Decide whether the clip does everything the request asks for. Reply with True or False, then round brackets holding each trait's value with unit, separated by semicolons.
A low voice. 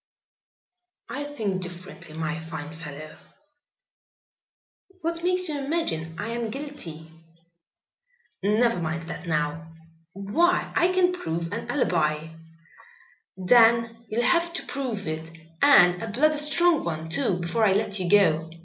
False (200 Hz)